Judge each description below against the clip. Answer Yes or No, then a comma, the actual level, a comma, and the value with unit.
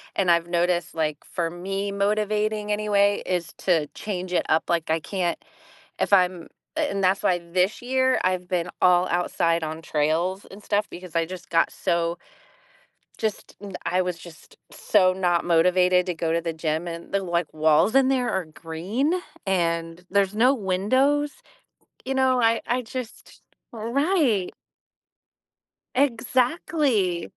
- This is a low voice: No, medium, 185 Hz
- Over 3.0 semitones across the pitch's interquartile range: Yes, average, 3.9 semitones